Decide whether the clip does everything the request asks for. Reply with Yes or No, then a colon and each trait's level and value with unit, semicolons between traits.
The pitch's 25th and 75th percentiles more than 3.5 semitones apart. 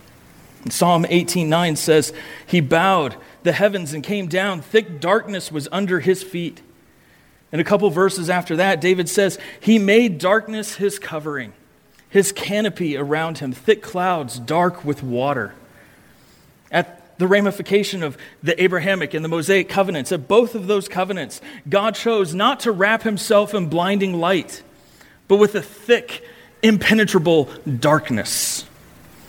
Yes: average, 4.0 semitones